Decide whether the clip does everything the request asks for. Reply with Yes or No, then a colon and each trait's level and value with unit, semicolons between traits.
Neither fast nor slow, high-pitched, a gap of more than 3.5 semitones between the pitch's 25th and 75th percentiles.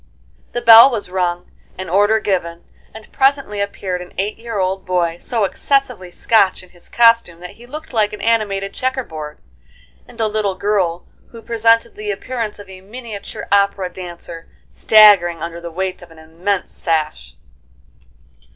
Yes: average, 160 wpm; high, 200 Hz; average, 4.2 semitones